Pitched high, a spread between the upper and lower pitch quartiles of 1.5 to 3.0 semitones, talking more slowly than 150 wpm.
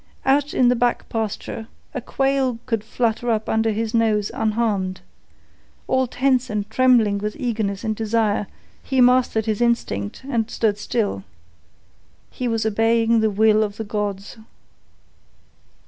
Yes: high, 225 Hz; narrow, 2.4 semitones; average, 140 wpm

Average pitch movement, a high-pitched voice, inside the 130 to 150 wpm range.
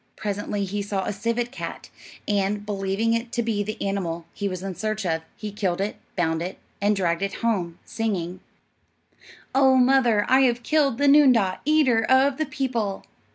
No: average, 4.0 semitones; high, 210 Hz; average, 175 wpm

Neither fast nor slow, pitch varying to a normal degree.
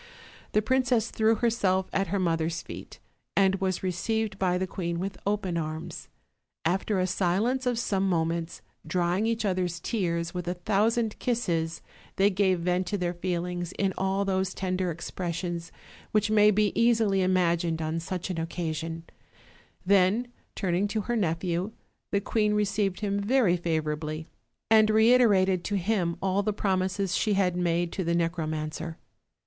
Yes: average, 160 wpm; average, 3.2 semitones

